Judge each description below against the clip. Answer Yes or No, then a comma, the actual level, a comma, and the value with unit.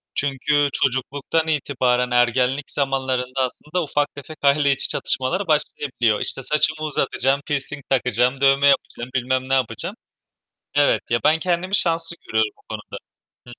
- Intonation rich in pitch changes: No, average, 2.7 semitones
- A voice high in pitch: No, low, 135 Hz